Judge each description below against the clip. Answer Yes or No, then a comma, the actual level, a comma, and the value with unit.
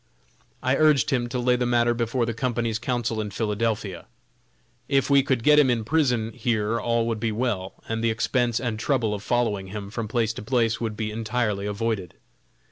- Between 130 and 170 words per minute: No, average, 195 wpm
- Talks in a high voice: No, low, 115 Hz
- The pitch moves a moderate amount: No, narrow, 2.2 semitones